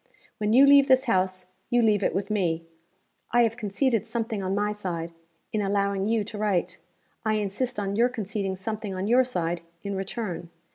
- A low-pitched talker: No, high, 205 Hz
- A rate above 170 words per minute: Yes, average, 185 wpm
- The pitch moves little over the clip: No, average, 3.1 semitones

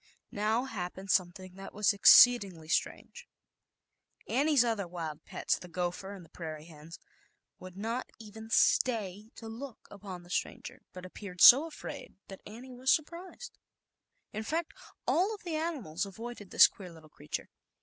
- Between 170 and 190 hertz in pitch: No, high, 205 Hz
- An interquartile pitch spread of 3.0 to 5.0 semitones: No, wide, 5.5 semitones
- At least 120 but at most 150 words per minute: No, average, 160 wpm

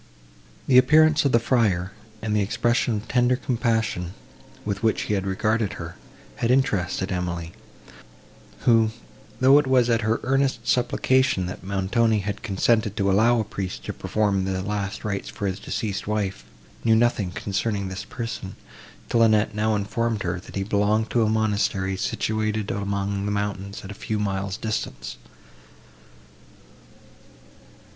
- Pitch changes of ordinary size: Yes, average, 3.0 semitones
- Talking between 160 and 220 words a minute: No, average, 150 wpm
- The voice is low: Yes, low, 105 Hz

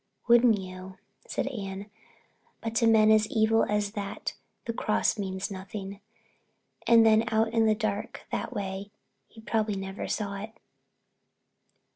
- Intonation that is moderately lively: No, narrow, 2.1 semitones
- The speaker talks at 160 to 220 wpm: No, average, 140 wpm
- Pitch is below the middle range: No, high, 215 Hz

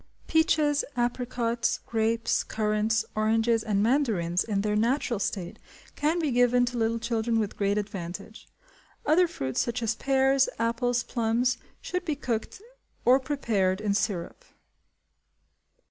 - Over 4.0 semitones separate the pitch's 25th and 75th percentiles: No, average, 3.2 semitones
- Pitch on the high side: Yes, high, 230 Hz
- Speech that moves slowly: Yes, slow, 130 wpm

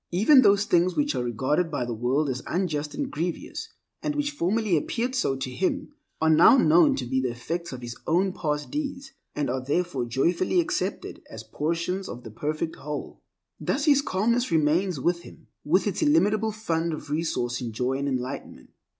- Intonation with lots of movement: Yes, wide, 7.4 semitones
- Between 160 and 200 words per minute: Yes, average, 185 wpm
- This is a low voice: No, medium, 165 Hz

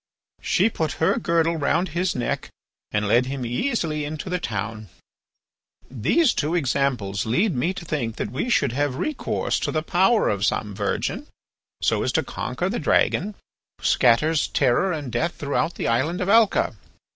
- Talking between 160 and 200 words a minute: Yes, average, 170 wpm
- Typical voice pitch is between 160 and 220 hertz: No, medium, 145 Hz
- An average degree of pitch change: No, wide, 6.6 semitones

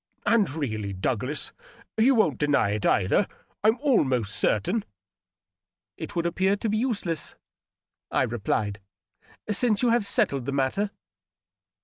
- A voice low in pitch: No, medium, 150 Hz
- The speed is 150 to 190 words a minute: No, slow, 135 wpm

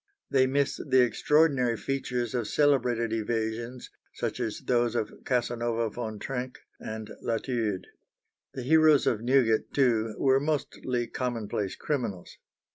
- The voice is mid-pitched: No, low, 120 Hz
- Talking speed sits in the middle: No, slow, 120 wpm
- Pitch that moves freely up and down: No, average, 2.9 semitones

